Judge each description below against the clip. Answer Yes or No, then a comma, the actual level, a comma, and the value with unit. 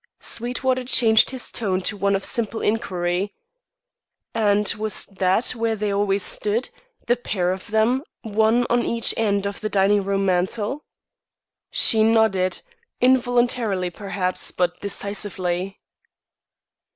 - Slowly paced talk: Yes, slow, 125 wpm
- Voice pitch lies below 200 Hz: No, high, 210 Hz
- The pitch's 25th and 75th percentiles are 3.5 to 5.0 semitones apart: No, average, 2.9 semitones